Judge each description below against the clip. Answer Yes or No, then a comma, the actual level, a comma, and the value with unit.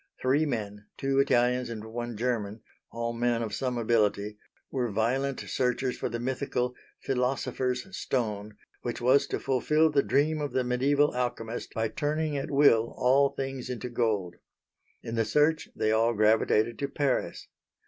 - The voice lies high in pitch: No, low, 125 Hz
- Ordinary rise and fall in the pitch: Yes, average, 3.2 semitones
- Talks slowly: No, average, 155 wpm